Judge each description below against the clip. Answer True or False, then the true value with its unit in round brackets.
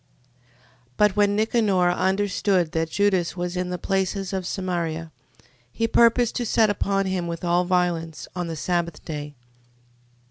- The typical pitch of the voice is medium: True (180 Hz)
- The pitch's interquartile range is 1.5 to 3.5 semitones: True (2.8 semitones)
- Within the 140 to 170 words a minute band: True (150 wpm)